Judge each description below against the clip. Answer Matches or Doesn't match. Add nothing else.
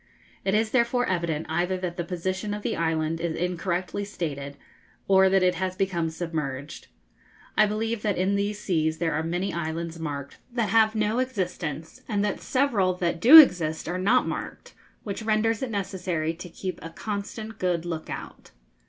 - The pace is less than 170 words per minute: Doesn't match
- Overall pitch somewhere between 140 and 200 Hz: Matches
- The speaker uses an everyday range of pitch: Matches